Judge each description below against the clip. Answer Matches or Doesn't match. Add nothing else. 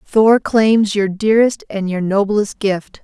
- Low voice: Doesn't match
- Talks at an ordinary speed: Matches